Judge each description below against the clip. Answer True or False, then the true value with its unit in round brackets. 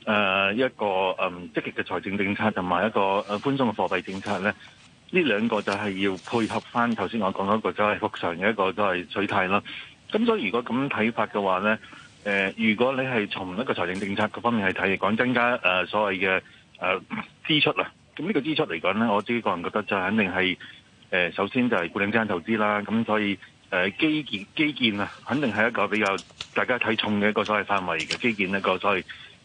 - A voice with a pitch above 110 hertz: False (105 Hz)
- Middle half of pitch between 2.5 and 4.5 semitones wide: True (3.2 semitones)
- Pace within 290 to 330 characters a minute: True (325 characters per minute)